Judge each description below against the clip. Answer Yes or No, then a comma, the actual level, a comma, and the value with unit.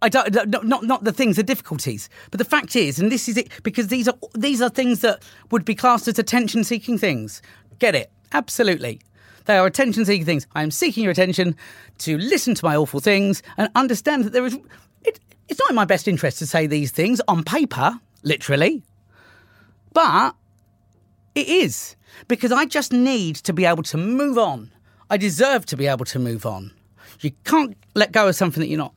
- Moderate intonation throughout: No, wide, 8.7 semitones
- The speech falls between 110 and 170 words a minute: No, fast, 205 wpm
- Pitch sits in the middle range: No, high, 205 Hz